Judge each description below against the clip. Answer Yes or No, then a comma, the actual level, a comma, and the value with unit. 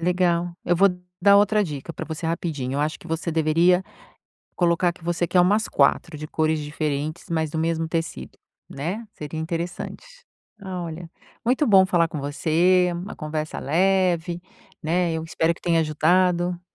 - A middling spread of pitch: No, narrow, 2.2 semitones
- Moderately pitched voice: Yes, medium, 170 Hz